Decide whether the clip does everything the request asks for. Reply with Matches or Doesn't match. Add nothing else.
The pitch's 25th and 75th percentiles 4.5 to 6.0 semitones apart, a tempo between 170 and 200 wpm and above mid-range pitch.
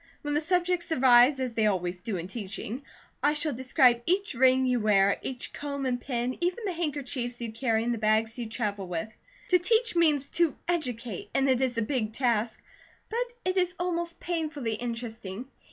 Matches